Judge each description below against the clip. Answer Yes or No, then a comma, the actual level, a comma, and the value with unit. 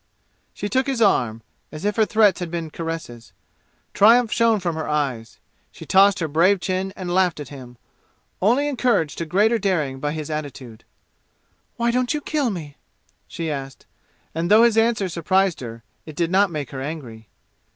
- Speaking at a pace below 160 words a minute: No, average, 175 wpm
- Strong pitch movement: Yes, wide, 6.2 semitones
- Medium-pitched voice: Yes, medium, 175 Hz